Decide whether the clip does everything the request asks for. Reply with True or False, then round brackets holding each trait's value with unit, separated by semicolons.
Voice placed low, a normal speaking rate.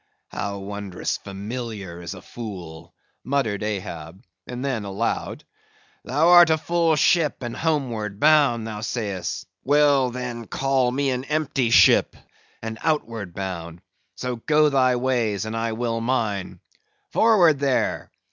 False (120 Hz; 130 wpm)